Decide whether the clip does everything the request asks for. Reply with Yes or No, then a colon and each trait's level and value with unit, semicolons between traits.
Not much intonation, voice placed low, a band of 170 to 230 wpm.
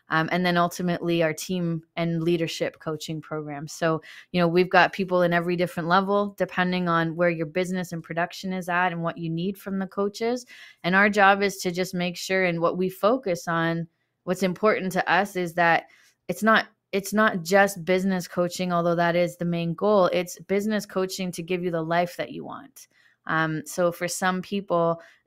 No: narrow, 2.0 semitones; medium, 175 Hz; average, 200 wpm